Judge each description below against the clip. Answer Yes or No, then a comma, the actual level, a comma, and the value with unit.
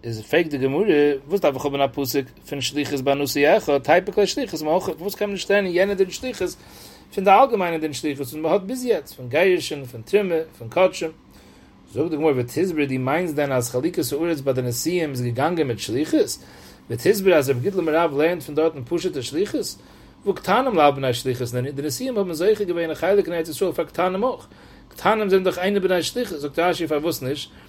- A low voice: No, medium, 160 Hz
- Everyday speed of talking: No, fast, 215 wpm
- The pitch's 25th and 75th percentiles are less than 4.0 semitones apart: No, average, 5.1 semitones